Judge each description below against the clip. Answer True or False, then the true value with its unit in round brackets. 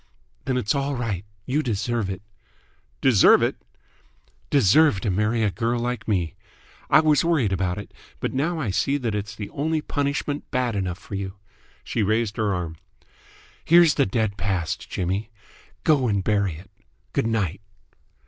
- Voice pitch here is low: True (110 Hz)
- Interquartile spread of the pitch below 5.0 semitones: False (5.5 semitones)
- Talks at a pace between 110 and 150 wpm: False (160 wpm)